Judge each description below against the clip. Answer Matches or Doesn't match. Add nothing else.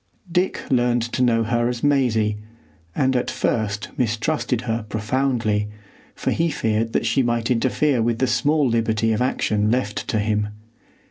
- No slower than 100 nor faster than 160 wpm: Matches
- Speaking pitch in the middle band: Doesn't match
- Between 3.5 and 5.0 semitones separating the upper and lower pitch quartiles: Doesn't match